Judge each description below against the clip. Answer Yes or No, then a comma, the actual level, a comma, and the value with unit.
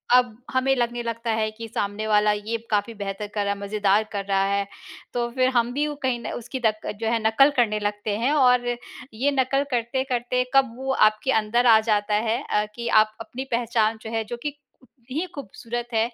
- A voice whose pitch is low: No, high, 230 Hz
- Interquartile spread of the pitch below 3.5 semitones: Yes, average, 2.9 semitones